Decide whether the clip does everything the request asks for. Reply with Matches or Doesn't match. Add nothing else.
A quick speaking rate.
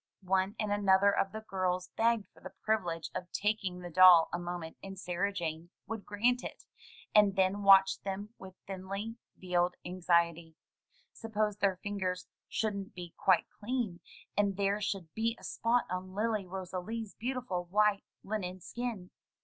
Doesn't match